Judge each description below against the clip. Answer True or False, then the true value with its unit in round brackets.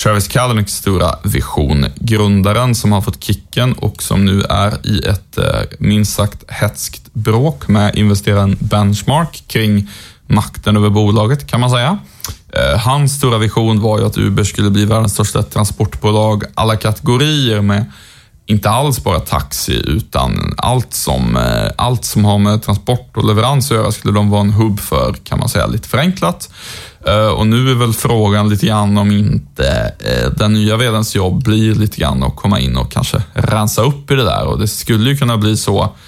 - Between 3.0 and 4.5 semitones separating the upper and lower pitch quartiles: False (2.4 semitones)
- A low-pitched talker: True (105 Hz)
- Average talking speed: True (175 wpm)